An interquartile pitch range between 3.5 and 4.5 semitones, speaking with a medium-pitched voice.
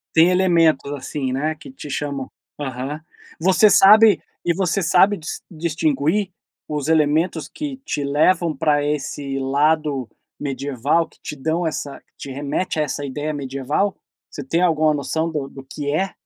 No: average, 3.0 semitones; medium, 150 Hz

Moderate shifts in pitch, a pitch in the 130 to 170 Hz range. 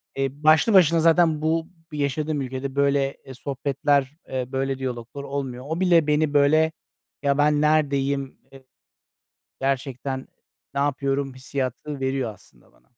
No: narrow, 2.1 semitones; medium, 140 Hz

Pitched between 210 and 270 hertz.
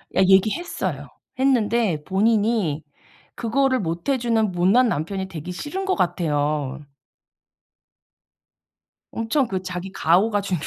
No: high, 195 Hz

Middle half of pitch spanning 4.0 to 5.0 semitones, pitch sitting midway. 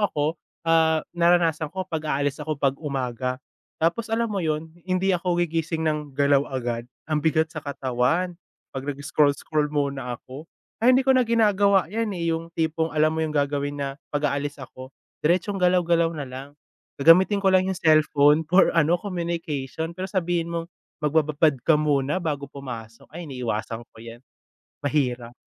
No: average, 3.4 semitones; medium, 155 Hz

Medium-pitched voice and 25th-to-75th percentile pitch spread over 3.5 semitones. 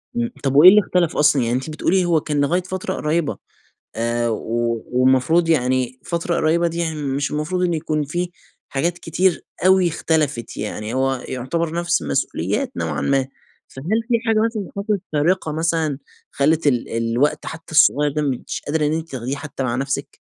Yes: medium, 150 Hz; average, 4.6 semitones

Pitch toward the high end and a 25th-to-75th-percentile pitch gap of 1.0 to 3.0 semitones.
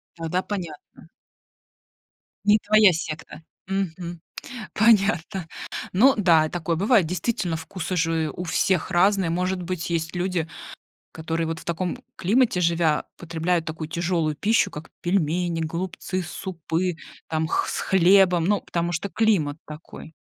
No: medium, 175 Hz; average, 2.7 semitones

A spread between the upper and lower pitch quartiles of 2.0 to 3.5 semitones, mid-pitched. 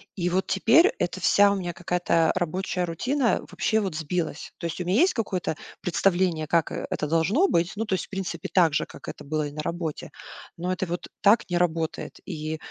Yes: average, 2.9 semitones; medium, 180 Hz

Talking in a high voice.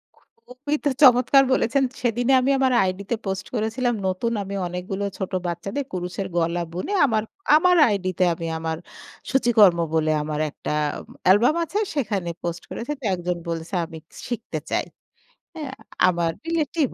Yes: high, 205 Hz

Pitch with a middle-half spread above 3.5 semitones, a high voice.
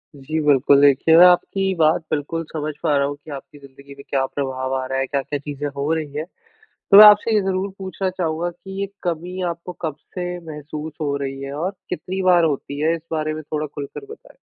No: average, 4.0 semitones; medium, 155 Hz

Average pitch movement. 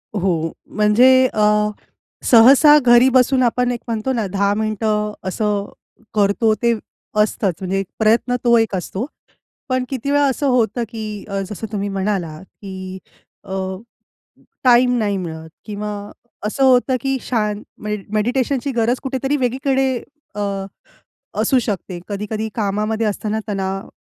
Yes: average, 3.6 semitones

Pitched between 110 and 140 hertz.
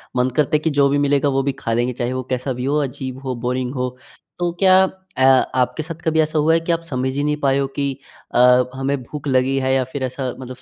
Yes: low, 135 Hz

